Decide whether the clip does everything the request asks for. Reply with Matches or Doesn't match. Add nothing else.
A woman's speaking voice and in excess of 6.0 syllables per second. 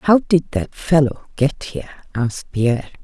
Doesn't match